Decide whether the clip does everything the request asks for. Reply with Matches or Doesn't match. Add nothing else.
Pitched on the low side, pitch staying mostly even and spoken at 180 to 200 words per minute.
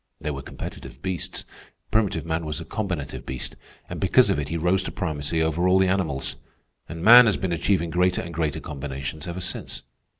Doesn't match